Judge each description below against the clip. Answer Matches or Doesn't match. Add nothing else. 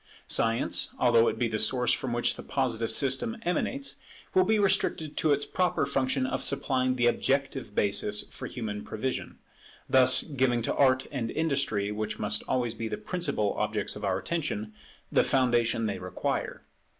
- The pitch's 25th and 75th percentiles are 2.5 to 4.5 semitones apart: Matches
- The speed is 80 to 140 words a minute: Doesn't match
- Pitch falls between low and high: Doesn't match